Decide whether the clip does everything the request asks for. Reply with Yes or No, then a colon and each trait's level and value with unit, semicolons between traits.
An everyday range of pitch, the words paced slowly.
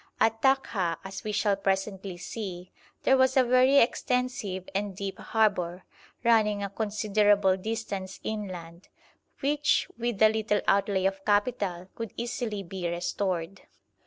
Yes: average, 3.0 semitones; slow, 130 wpm